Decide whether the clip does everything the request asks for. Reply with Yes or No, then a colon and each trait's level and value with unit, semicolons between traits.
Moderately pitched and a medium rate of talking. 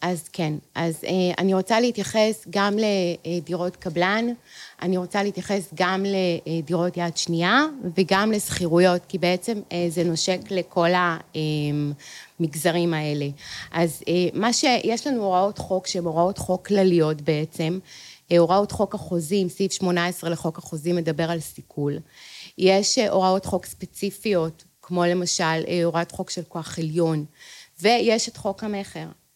Yes: medium, 180 Hz; average, 125 wpm